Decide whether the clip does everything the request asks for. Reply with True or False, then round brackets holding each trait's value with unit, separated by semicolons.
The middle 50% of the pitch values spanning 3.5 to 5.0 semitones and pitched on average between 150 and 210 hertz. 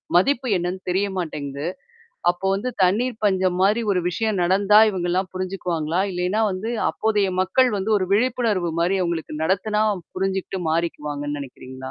False (3.0 semitones; 185 Hz)